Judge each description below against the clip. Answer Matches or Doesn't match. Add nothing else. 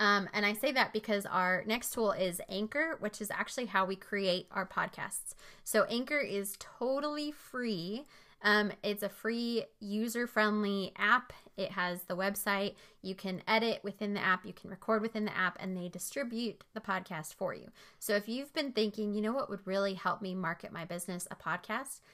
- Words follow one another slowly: Doesn't match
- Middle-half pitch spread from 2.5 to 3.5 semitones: Matches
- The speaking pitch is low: Doesn't match